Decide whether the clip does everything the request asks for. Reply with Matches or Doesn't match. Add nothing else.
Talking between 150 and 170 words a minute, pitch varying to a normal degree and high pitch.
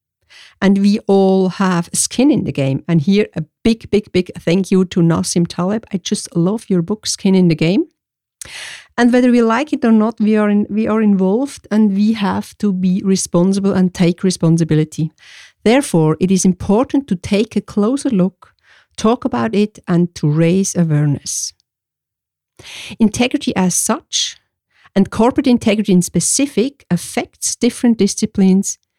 Matches